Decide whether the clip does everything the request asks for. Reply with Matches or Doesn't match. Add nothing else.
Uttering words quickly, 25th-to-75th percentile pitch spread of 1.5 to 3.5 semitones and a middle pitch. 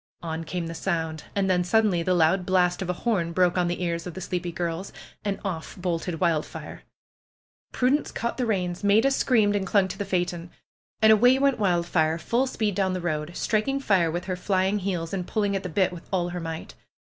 Matches